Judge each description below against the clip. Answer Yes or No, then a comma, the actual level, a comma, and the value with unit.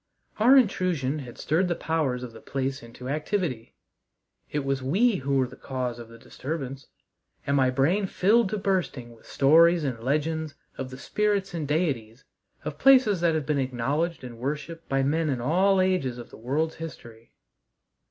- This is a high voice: No, medium, 145 Hz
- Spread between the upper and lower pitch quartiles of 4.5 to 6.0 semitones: Yes, average, 5.1 semitones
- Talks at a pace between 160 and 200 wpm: Yes, average, 175 wpm